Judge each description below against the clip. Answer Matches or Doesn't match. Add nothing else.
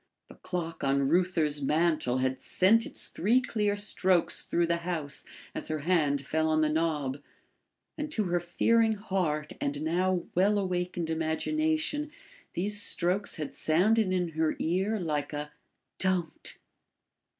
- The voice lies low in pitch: Doesn't match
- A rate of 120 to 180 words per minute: Matches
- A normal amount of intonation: Matches